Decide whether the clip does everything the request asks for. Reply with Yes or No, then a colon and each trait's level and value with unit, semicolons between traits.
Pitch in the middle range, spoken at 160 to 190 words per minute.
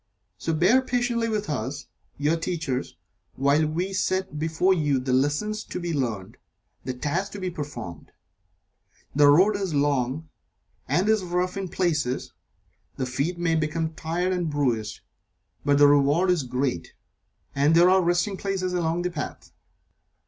No: medium, 160 Hz; average, 150 wpm